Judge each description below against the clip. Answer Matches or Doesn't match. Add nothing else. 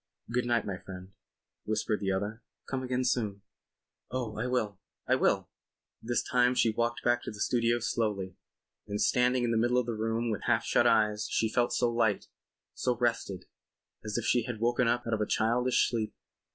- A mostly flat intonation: Matches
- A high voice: Doesn't match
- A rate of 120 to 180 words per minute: Doesn't match